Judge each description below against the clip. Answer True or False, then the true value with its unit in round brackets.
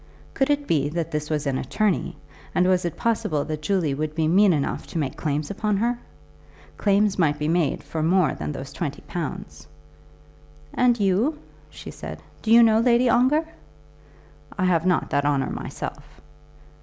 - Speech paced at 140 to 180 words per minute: True (170 wpm)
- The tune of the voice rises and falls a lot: True (6.0 semitones)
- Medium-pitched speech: True (175 Hz)